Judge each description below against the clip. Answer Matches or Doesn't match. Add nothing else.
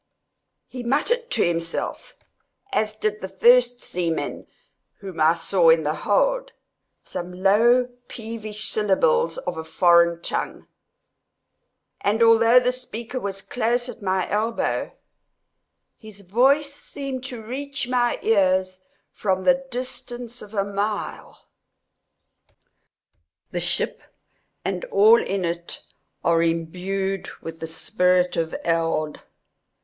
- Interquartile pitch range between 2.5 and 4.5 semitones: Doesn't match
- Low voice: Doesn't match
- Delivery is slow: Matches